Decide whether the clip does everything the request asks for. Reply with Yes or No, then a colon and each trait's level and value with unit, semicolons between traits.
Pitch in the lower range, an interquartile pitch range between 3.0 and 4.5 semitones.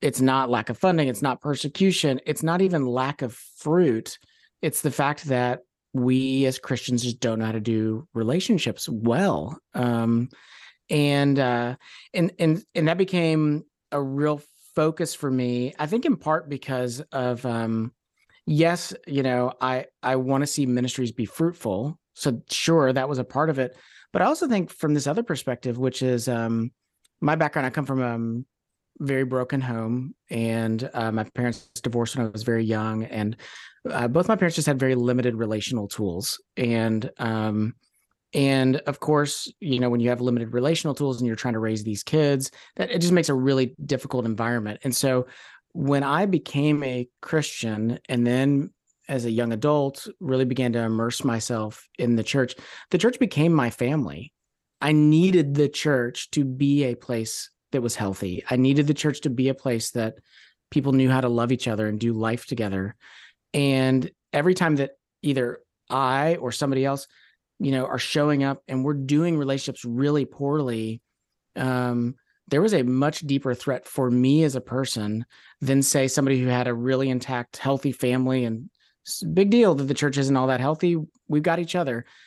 Yes: low, 130 Hz; average, 3.5 semitones